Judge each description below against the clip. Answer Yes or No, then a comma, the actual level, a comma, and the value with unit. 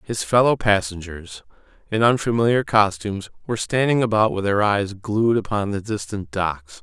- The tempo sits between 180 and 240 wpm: No, average, 150 wpm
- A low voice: Yes, low, 105 Hz